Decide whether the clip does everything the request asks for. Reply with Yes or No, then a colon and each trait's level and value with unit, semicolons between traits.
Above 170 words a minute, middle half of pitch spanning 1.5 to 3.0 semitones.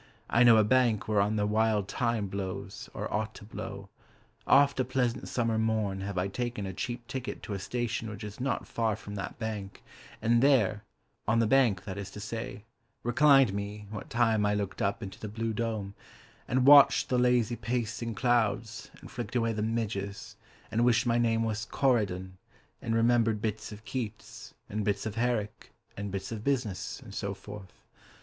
Yes: average, 185 wpm; average, 2.7 semitones